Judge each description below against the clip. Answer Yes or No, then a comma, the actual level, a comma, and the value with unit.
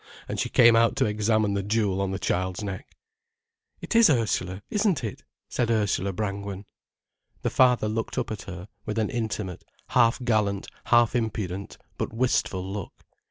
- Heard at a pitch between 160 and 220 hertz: No, low, 105 Hz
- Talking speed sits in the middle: Yes, average, 160 wpm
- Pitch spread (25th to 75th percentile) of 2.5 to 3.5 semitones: Yes, average, 2.9 semitones